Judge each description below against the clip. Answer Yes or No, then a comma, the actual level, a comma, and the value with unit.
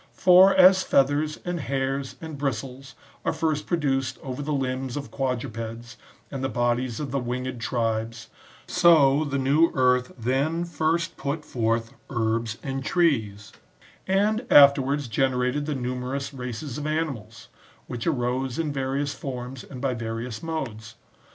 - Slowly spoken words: No, average, 145 wpm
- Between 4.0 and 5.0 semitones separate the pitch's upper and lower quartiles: No, average, 3.3 semitones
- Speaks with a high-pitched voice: No, low, 135 Hz